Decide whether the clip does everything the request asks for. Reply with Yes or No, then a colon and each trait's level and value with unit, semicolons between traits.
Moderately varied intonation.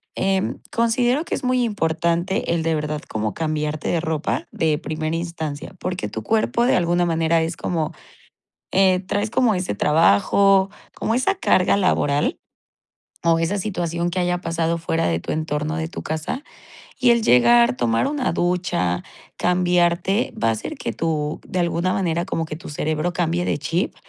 Yes: average, 3.2 semitones